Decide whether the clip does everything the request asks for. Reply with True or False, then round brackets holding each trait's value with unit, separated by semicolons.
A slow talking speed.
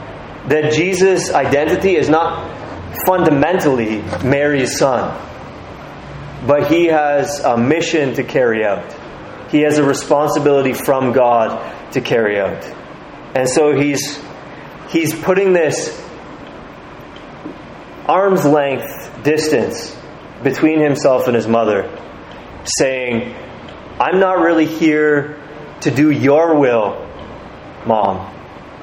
True (100 wpm)